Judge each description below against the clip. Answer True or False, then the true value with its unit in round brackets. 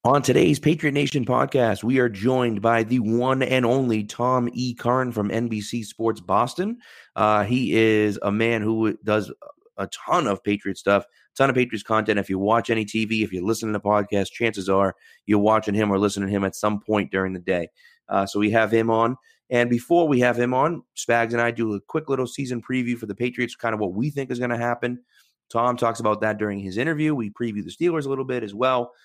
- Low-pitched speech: True (115 Hz)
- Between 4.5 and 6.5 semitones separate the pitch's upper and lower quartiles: False (2.9 semitones)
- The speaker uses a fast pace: True (230 wpm)